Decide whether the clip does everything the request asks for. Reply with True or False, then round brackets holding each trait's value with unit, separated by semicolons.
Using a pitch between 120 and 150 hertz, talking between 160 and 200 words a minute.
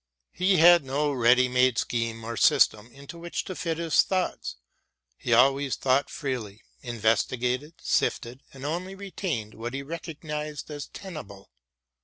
False (135 Hz; 140 wpm)